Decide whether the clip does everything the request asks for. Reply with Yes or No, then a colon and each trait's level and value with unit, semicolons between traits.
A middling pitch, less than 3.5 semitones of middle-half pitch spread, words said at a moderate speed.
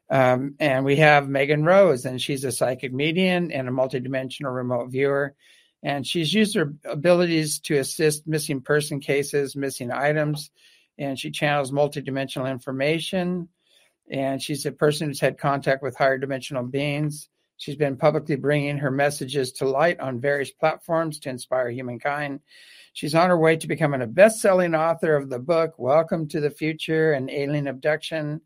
Yes: medium, 145 Hz; narrow, 2.6 semitones; average, 165 wpm